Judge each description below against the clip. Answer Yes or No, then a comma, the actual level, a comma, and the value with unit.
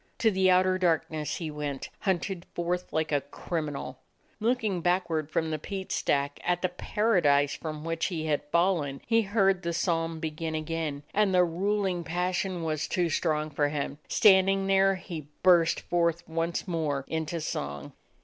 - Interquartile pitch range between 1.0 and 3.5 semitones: Yes, average, 3.2 semitones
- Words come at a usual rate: Yes, average, 160 wpm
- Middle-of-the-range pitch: Yes, medium, 170 Hz